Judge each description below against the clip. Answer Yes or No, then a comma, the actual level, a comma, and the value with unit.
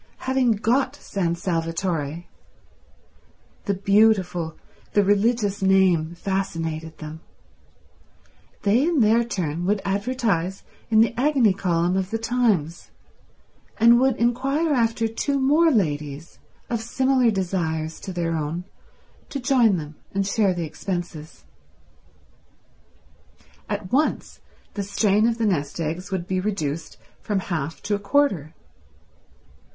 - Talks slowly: Yes, slow, 115 wpm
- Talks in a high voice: Yes, high, 195 Hz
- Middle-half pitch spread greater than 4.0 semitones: Yes, wide, 5.5 semitones